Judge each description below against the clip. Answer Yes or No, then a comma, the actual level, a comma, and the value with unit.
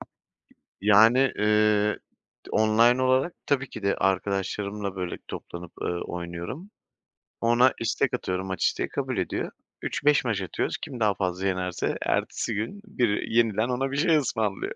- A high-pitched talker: No, low, 110 Hz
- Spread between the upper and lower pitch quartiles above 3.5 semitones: Yes, average, 4.7 semitones